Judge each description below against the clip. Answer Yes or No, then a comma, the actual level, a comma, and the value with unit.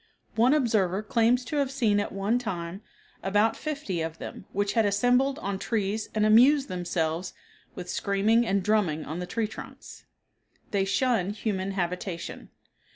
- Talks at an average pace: Yes, average, 155 wpm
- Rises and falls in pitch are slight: No, average, 3.7 semitones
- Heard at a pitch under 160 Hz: No, high, 205 Hz